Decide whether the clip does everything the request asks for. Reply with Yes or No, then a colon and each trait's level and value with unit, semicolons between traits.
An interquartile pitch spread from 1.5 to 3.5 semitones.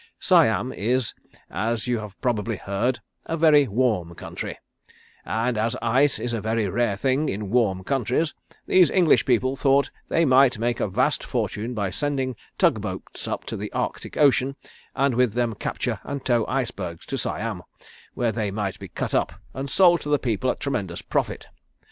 No: average, 4.0 semitones